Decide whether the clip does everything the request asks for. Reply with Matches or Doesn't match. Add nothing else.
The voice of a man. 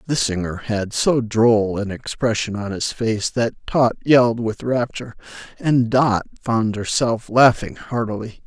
Matches